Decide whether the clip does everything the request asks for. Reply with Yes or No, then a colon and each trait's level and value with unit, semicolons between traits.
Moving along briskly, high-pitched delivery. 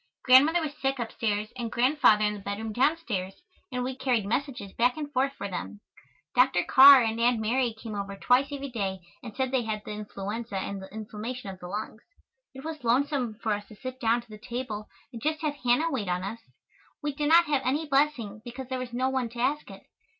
Yes: fast, 215 wpm; high, 240 Hz